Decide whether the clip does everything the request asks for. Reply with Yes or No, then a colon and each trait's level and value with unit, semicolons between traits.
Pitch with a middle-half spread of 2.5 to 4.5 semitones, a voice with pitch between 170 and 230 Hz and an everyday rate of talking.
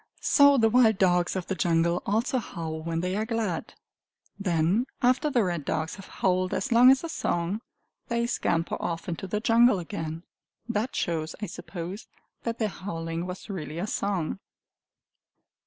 No: average, 5.3 semitones; high, 190 Hz; average, 165 wpm